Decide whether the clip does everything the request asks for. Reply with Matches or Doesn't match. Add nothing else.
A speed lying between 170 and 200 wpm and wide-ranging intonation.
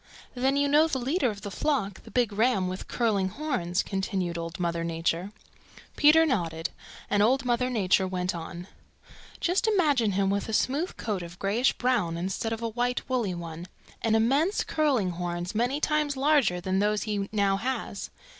Matches